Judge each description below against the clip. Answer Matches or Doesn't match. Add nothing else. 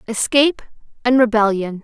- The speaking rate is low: Matches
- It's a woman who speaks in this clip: Matches